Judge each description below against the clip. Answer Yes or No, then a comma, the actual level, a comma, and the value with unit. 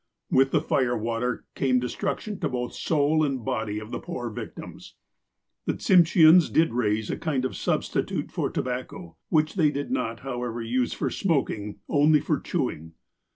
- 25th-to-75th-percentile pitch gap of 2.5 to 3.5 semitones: No, average, 4.6 semitones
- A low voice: Yes, low, 130 Hz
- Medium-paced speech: Yes, average, 165 wpm